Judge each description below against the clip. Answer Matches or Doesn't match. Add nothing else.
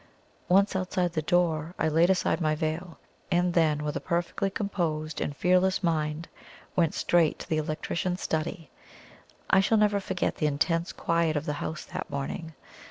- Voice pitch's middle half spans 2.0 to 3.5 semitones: Matches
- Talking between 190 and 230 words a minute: Doesn't match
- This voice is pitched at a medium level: Matches